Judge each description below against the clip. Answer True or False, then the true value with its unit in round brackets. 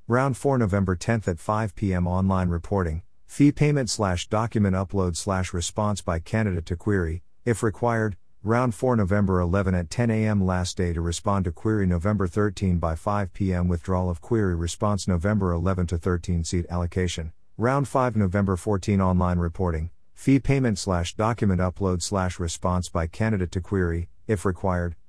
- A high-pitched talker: False (95 Hz)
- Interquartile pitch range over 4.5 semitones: False (3.3 semitones)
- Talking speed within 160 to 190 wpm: True (165 wpm)